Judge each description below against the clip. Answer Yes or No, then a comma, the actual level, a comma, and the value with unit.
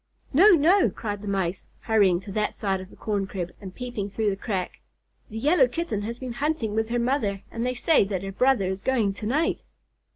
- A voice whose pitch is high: Yes, high, 215 Hz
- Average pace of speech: No, fast, 220 wpm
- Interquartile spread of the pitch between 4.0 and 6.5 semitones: Yes, average, 4.4 semitones